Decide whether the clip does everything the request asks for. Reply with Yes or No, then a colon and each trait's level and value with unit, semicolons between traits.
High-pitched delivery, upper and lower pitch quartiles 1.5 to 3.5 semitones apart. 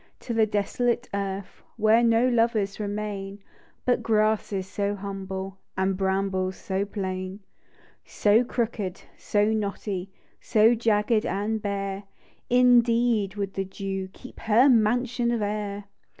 Yes: high, 205 Hz; average, 2.7 semitones